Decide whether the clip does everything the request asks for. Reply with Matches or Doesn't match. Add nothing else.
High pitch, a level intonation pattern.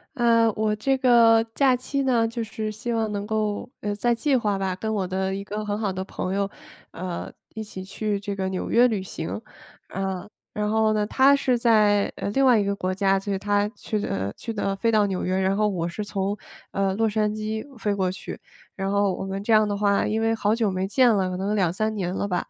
Matches